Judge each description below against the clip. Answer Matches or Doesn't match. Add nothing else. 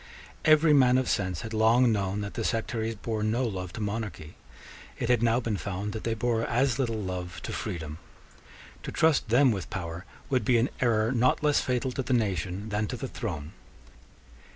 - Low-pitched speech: Matches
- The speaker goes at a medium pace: Matches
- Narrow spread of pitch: Doesn't match